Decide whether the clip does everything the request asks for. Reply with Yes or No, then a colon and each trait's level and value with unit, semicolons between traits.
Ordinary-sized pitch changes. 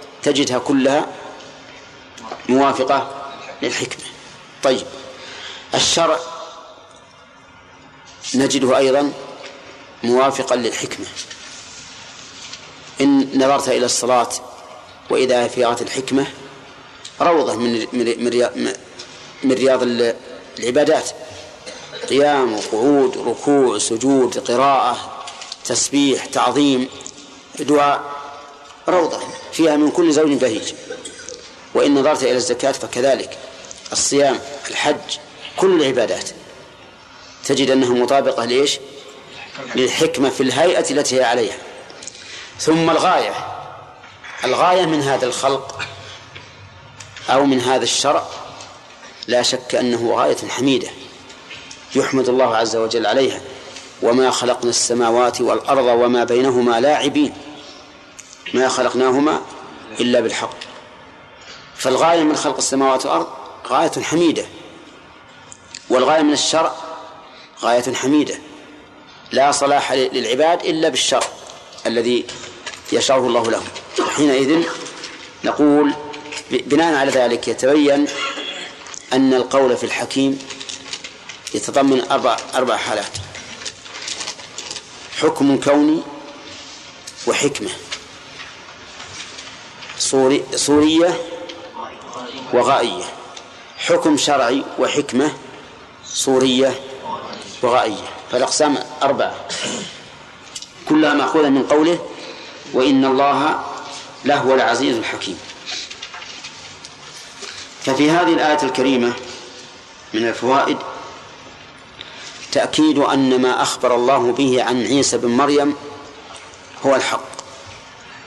No: narrow, 2.3 semitones